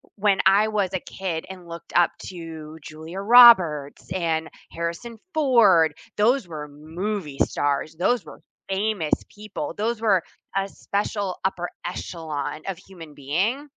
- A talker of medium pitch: Yes, medium, 180 Hz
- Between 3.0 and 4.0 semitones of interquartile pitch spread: No, average, 4.5 semitones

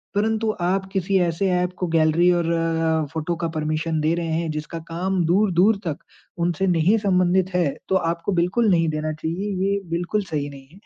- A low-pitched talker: No, medium, 175 Hz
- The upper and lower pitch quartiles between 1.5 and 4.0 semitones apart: Yes, average, 2.9 semitones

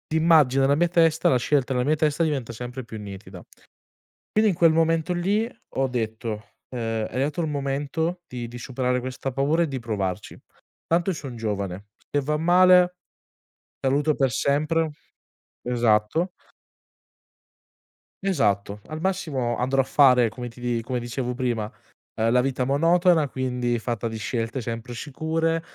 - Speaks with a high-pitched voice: No, low, 130 Hz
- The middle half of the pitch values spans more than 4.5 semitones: Yes, average, 5.2 semitones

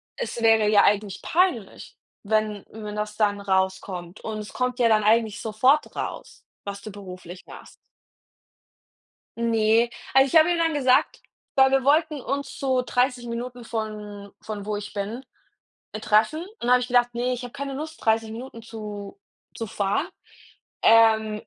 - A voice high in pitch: Yes, high, 225 Hz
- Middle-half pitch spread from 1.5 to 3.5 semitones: Yes, average, 3.2 semitones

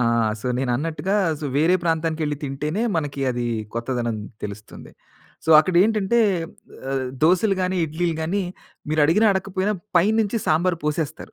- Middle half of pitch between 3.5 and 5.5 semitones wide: Yes, average, 4.4 semitones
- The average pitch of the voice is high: No, medium, 160 Hz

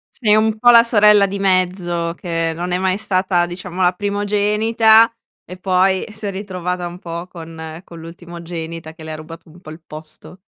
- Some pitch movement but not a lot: Yes, average, 3.2 semitones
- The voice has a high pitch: No, medium, 180 Hz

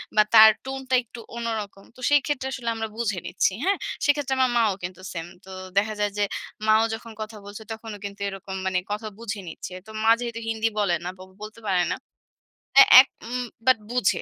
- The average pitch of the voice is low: No, high, 220 Hz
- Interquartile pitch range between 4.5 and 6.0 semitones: No, average, 3.1 semitones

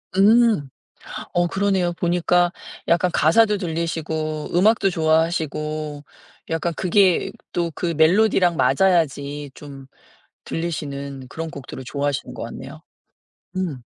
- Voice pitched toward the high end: No, medium, 165 Hz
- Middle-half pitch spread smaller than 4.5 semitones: Yes, average, 3.4 semitones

